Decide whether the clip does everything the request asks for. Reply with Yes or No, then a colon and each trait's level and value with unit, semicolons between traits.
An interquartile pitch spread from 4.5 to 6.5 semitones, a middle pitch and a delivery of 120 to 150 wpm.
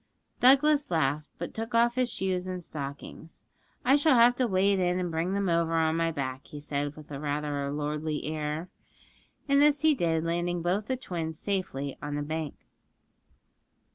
No: average, 5.2 semitones; medium, 165 Hz; average, 175 wpm